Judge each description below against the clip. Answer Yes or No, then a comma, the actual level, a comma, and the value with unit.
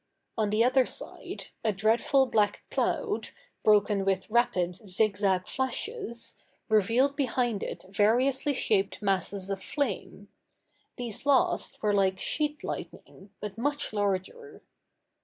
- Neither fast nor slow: No, slow, 120 wpm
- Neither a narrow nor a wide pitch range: Yes, average, 4.8 semitones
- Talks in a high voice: Yes, high, 215 Hz